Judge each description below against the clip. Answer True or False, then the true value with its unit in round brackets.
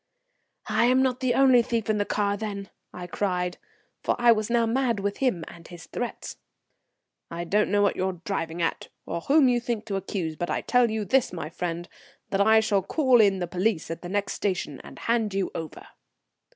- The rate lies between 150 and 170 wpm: False (205 wpm)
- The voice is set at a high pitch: True (205 Hz)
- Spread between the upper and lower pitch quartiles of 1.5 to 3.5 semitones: False (4.7 semitones)